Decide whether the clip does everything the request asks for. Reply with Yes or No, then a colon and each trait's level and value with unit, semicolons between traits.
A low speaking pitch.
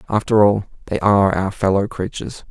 Yes: low, 100 Hz